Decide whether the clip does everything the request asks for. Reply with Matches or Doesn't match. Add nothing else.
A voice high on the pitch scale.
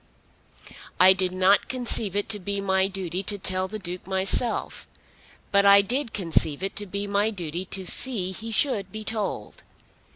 Matches